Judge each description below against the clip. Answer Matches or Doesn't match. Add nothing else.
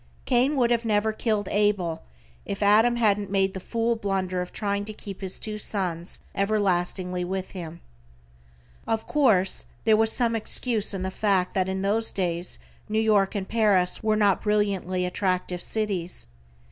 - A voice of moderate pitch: Doesn't match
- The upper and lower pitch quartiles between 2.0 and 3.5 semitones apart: Matches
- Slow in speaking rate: Doesn't match